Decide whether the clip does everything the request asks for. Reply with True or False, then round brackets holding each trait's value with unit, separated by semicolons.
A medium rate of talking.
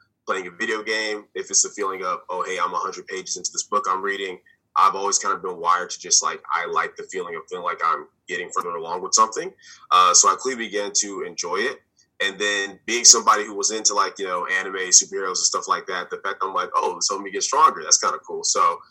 False (255 wpm)